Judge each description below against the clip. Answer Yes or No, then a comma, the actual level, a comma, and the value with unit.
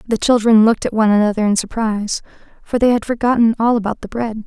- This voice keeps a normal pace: No, fast, 215 wpm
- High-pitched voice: Yes, high, 220 Hz